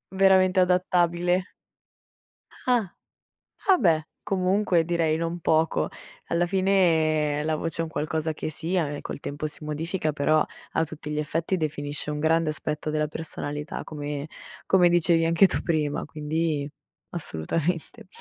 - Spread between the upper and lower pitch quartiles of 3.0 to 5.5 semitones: No, narrow, 2.6 semitones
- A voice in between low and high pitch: Yes, medium, 160 Hz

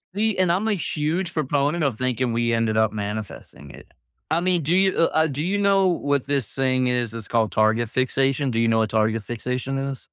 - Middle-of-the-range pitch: No, low, 130 Hz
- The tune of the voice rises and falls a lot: Yes, wide, 6.0 semitones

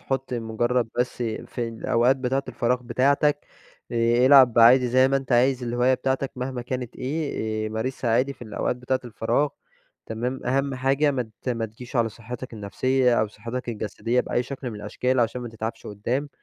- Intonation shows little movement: Yes, narrow, 2.2 semitones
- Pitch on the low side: Yes, low, 125 Hz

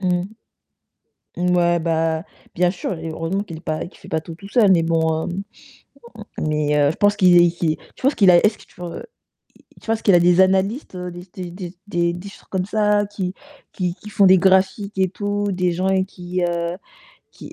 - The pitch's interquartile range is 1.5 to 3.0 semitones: Yes, narrow, 2.4 semitones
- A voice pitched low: No, medium, 180 Hz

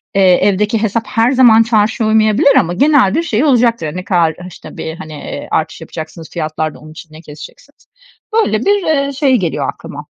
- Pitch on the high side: Yes, high, 210 Hz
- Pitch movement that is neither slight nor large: No, wide, 7.2 semitones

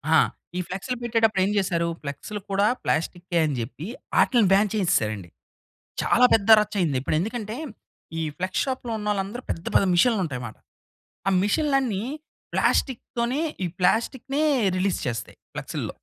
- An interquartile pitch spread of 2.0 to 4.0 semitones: No, wide, 5.4 semitones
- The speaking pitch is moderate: No, high, 200 Hz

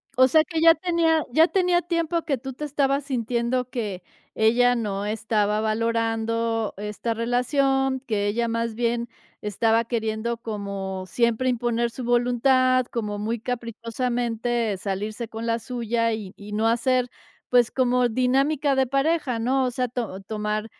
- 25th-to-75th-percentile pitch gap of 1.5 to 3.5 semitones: Yes, narrow, 2.6 semitones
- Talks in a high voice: Yes, high, 235 Hz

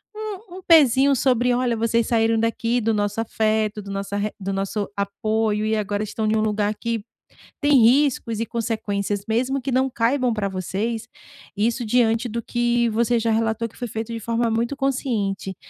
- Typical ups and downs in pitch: No, narrow, 2.3 semitones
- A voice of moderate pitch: No, high, 225 Hz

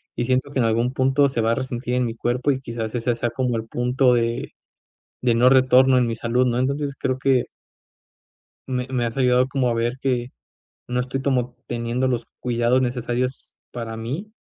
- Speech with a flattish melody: Yes, narrow, 1.6 semitones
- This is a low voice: Yes, low, 125 Hz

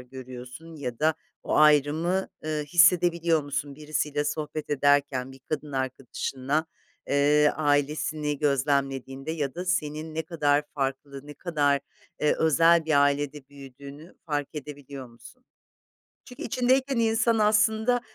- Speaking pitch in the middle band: Yes, medium, 150 Hz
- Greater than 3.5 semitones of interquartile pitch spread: No, narrow, 2.6 semitones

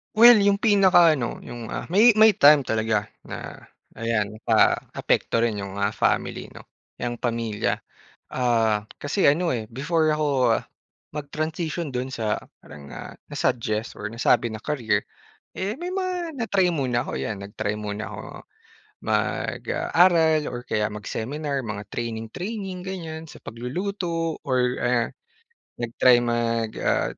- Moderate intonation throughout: No, wide, 7.6 semitones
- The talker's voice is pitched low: Yes, low, 130 Hz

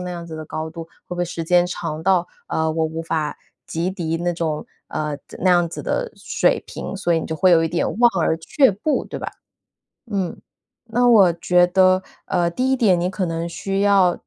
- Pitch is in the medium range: Yes, medium, 175 Hz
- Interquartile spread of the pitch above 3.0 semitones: No, narrow, 2.6 semitones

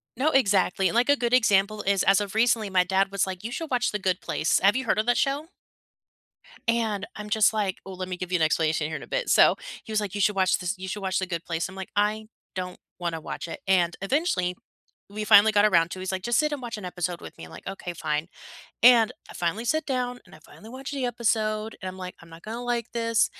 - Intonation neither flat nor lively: Yes, average, 4.1 semitones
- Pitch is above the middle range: Yes, high, 205 Hz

